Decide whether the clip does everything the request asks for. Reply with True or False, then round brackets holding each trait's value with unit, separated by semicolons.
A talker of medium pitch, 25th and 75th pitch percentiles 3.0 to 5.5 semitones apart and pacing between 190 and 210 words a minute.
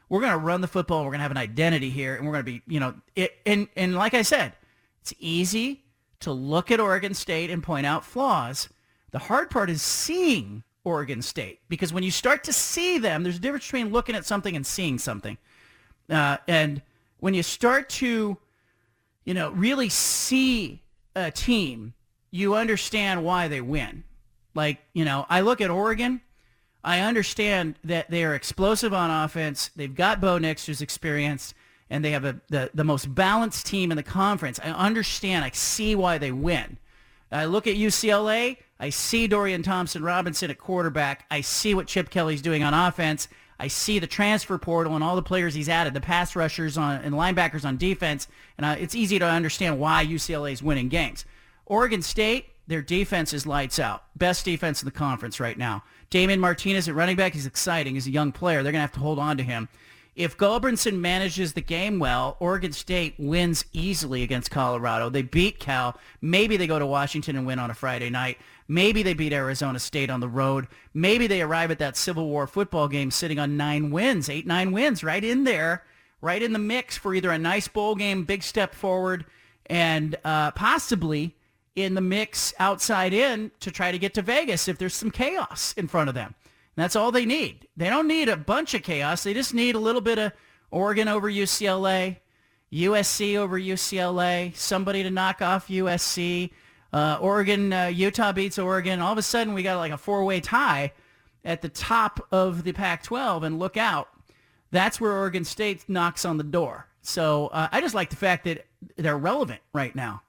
True (175 Hz; 5.2 semitones; 200 wpm)